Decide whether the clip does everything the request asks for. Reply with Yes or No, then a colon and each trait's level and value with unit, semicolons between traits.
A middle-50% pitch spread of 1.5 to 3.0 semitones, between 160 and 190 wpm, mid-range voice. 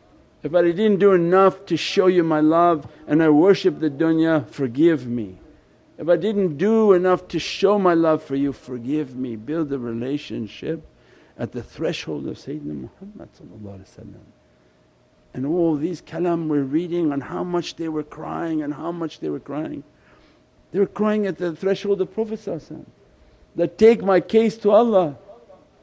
No: average, 4.4 semitones; average, 165 wpm; medium, 165 Hz